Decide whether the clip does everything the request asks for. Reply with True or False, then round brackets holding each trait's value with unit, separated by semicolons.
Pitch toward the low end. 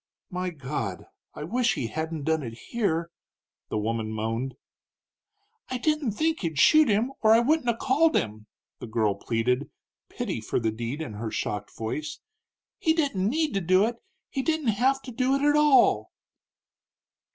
False (185 Hz)